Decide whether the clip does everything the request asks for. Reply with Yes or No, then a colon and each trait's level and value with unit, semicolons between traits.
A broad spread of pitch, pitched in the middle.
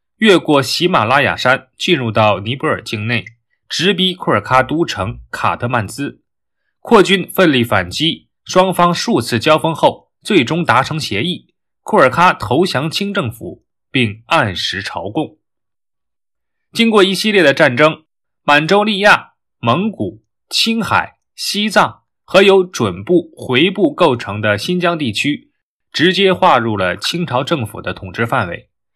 Yes: wide, 7.9 semitones; medium, 155 Hz